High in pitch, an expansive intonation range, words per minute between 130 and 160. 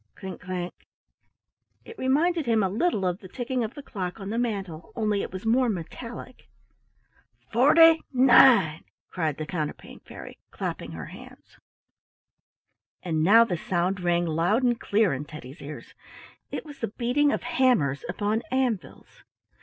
Yes: high, 210 Hz; wide, 6.1 semitones; average, 150 wpm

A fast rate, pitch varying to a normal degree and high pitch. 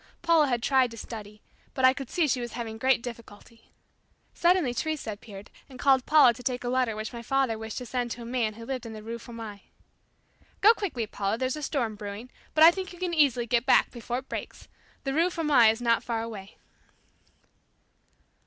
Yes: fast, 210 wpm; average, 3.2 semitones; high, 245 Hz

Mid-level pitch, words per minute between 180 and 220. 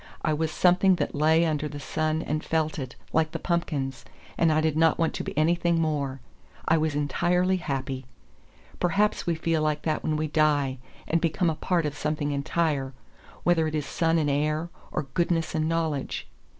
Yes: medium, 155 Hz; average, 190 wpm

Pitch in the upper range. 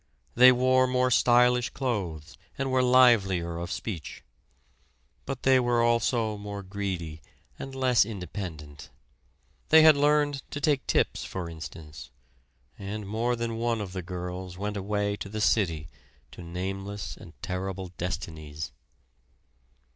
No: low, 100 Hz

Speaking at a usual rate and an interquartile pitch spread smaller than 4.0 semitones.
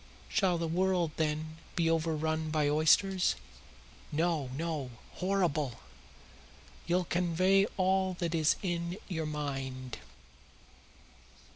No: slow, 100 wpm; average, 2.9 semitones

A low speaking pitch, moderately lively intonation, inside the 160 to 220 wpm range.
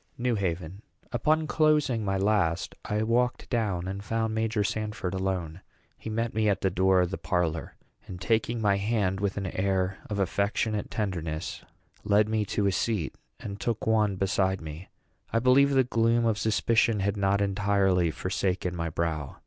Yes: low, 100 Hz; average, 3.1 semitones; average, 170 wpm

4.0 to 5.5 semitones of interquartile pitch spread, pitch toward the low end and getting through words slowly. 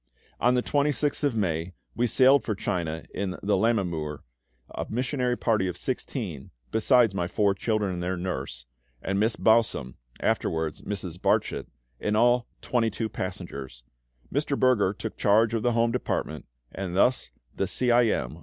No: average, 5.1 semitones; low, 105 Hz; average, 155 wpm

